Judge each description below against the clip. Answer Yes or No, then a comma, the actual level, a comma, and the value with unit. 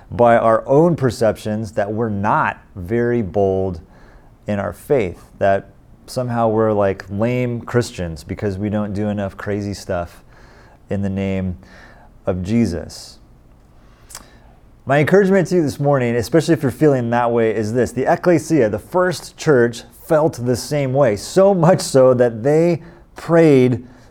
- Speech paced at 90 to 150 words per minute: Yes, average, 145 wpm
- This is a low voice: Yes, low, 120 Hz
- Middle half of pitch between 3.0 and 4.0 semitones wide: No, average, 5.2 semitones